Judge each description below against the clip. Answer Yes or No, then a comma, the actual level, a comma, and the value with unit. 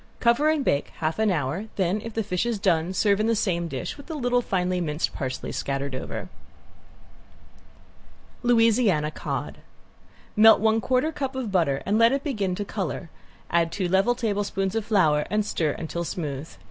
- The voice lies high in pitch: Yes, high, 200 Hz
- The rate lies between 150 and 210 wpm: Yes, average, 170 wpm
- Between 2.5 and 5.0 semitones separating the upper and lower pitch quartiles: No, wide, 5.4 semitones